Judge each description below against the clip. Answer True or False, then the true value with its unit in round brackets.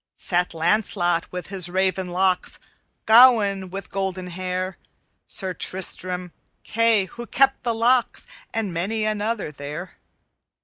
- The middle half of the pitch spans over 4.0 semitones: False (3.4 semitones)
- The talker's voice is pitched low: False (190 Hz)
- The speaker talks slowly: True (115 wpm)